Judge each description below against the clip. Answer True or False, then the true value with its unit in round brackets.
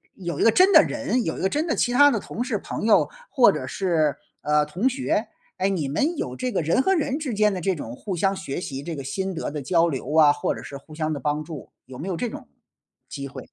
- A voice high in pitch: False (180 Hz)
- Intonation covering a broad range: True (8.0 semitones)